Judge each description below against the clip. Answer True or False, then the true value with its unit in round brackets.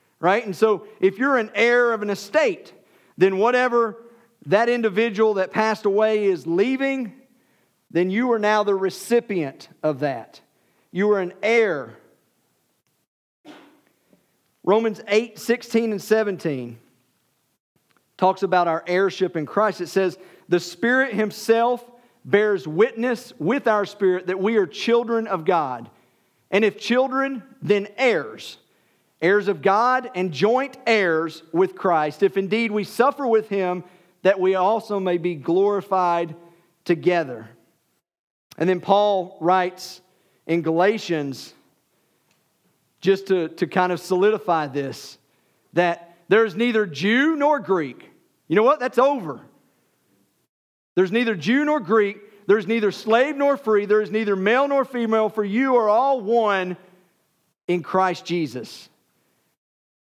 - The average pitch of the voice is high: True (205 Hz)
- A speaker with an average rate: False (130 wpm)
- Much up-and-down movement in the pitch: False (4.2 semitones)